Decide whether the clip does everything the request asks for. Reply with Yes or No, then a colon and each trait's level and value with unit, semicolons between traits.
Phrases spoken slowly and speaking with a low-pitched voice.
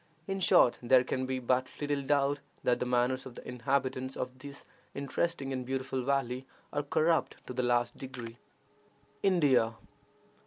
No: average, 155 wpm; low, 130 Hz